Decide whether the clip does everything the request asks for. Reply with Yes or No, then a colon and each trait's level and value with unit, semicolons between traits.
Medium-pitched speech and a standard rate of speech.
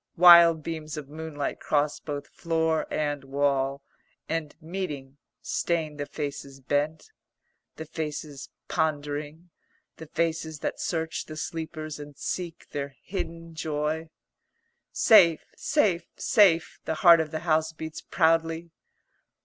No: medium, 160 Hz; slow, 120 wpm